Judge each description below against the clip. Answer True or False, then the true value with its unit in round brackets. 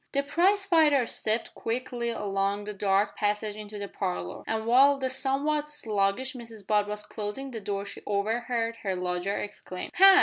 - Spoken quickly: False (170 wpm)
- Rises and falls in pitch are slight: False (4.7 semitones)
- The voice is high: True (220 Hz)